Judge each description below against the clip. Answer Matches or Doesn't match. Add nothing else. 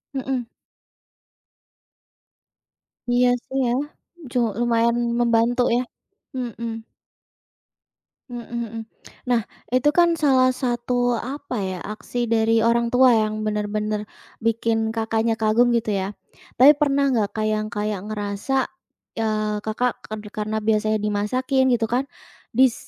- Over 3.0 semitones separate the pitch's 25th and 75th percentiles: Doesn't match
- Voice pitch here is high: Matches